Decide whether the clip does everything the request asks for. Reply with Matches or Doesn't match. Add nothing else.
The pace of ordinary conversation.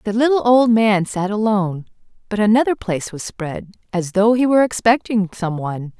Matches